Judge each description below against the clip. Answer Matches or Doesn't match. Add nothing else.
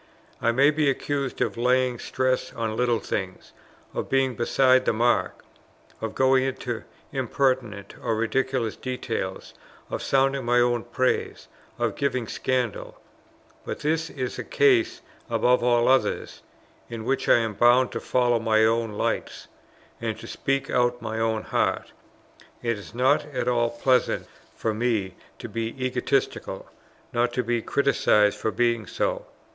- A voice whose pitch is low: Matches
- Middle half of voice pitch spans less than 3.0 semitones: Matches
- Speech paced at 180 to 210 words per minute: Doesn't match